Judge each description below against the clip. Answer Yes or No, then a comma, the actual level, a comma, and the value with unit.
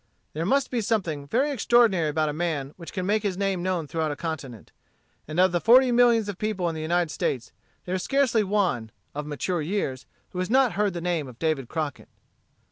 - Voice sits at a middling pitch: Yes, medium, 175 Hz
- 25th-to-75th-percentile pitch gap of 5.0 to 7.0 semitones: Yes, average, 5.3 semitones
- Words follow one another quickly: Yes, fast, 210 wpm